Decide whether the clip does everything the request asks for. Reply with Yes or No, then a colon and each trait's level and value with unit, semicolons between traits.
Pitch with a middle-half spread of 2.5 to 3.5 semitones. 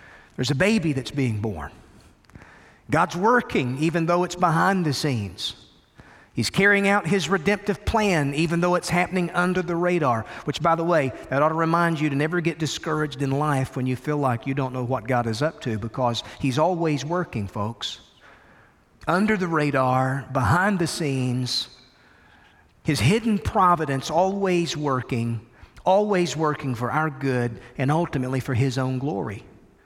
No: average, 5.1 semitones